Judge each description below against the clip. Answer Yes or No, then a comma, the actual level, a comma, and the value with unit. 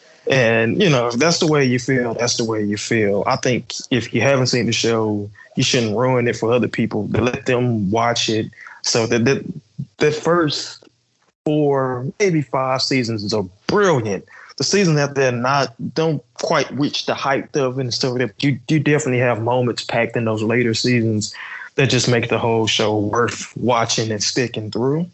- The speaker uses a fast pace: No, average, 190 wpm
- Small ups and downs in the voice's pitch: No, average, 3.4 semitones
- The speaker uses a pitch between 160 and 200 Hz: No, low, 125 Hz